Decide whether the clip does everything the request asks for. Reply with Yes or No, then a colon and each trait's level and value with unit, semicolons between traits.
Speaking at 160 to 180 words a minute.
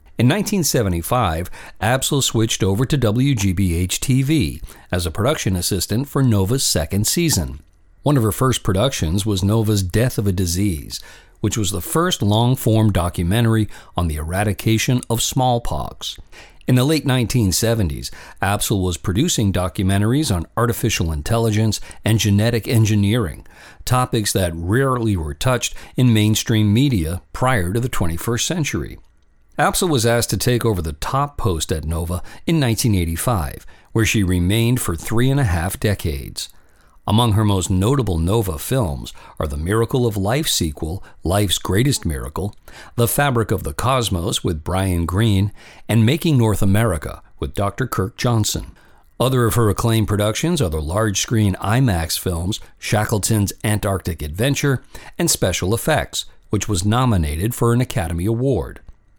No: average, 145 wpm